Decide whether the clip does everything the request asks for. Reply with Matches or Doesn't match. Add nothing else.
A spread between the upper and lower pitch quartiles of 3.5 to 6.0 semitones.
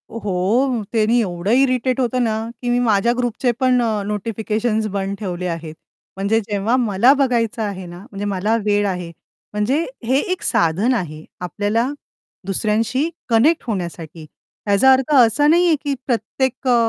Matches